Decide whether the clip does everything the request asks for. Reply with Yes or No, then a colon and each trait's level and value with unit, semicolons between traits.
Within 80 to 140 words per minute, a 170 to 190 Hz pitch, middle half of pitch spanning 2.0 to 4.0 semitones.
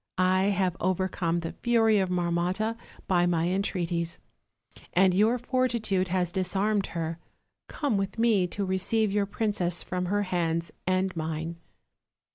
Yes: slow, 135 wpm; medium, 185 Hz; average, 2.9 semitones